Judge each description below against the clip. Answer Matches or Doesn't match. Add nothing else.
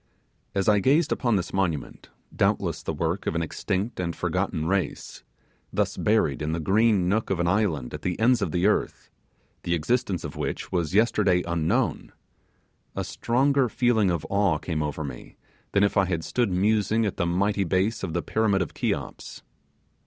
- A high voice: Doesn't match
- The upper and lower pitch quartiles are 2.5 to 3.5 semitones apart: Doesn't match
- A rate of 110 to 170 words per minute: Doesn't match